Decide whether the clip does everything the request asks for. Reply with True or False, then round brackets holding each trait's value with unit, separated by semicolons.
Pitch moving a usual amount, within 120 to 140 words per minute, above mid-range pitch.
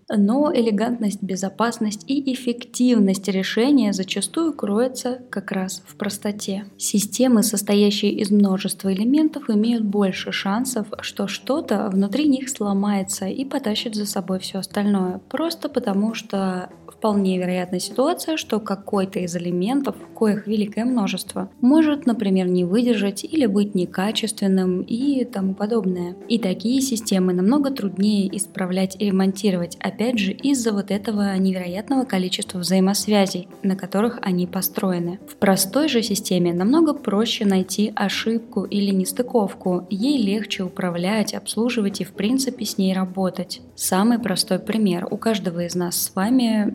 True (3.5 semitones; 135 wpm; 205 Hz)